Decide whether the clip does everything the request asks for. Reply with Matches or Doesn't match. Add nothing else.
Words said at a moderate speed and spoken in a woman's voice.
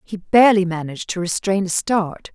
Matches